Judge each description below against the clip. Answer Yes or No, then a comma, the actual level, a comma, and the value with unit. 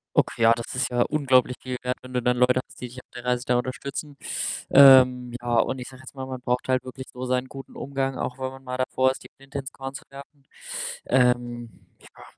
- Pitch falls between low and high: No, low, 130 Hz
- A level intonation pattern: Yes, narrow, 1.2 semitones